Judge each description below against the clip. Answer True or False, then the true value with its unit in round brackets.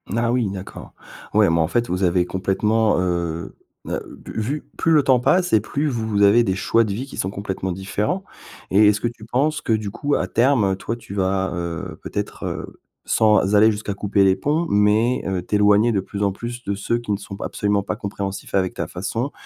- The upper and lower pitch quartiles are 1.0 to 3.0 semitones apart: False (3.5 semitones)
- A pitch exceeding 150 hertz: False (105 Hz)